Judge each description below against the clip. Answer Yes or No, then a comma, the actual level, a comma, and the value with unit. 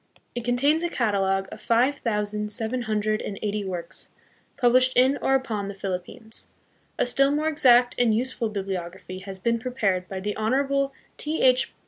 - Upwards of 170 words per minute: No, average, 165 wpm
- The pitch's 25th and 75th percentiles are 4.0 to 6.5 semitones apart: Yes, average, 4.4 semitones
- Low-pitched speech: No, high, 225 Hz